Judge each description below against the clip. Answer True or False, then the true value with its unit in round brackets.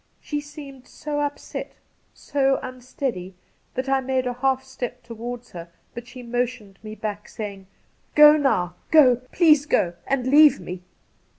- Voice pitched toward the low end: False (255 Hz)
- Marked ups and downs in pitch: False (3.3 semitones)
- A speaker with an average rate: True (160 wpm)